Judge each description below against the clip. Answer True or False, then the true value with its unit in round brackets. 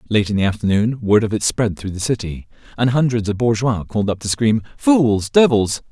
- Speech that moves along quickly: True (215 wpm)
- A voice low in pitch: True (110 Hz)